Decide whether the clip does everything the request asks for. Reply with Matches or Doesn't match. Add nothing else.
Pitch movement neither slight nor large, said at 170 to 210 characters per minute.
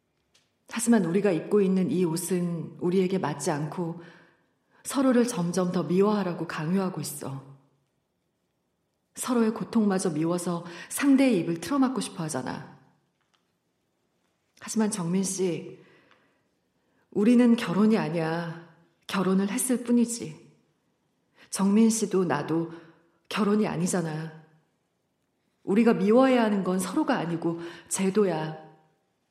Doesn't match